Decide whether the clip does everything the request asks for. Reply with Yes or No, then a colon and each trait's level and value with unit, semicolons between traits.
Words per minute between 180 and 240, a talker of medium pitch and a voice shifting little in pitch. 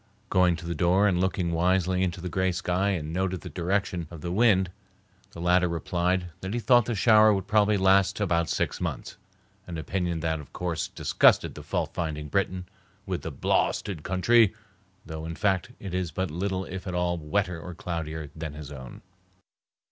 No: average, 185 wpm; very low, 90 Hz; narrow, 2.3 semitones